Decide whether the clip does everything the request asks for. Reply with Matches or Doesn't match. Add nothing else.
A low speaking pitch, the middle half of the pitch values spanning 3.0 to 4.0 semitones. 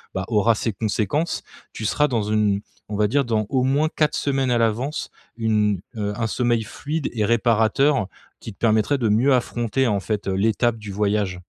Matches